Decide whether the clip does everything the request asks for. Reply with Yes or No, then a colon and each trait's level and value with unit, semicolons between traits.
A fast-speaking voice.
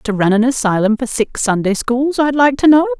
Yes: fast, 240 wpm